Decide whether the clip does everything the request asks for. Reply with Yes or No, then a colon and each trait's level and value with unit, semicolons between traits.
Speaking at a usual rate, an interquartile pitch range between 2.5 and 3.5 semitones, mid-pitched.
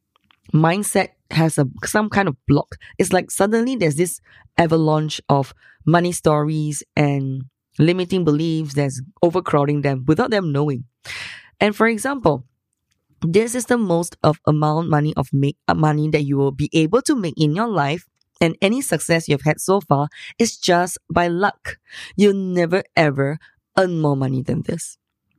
No: average, 160 wpm; average, 4.3 semitones; medium, 160 Hz